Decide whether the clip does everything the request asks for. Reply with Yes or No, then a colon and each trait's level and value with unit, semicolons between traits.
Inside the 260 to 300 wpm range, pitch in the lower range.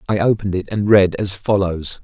No: fast, 205 wpm; low, 100 Hz